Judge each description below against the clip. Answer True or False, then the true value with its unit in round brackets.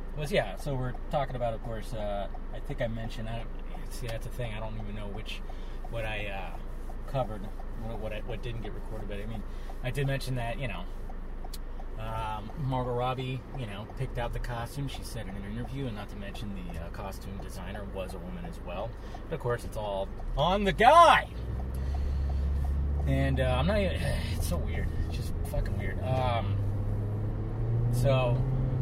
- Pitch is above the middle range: False (105 Hz)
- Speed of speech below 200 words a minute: True (190 wpm)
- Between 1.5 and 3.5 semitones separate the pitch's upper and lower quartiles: False (3.9 semitones)